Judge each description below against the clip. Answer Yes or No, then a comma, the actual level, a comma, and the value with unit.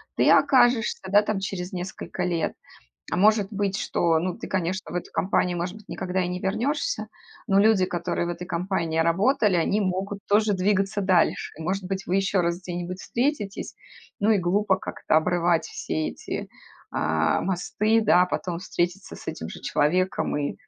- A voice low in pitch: No, medium, 185 Hz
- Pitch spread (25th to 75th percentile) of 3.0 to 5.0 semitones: No, narrow, 2.6 semitones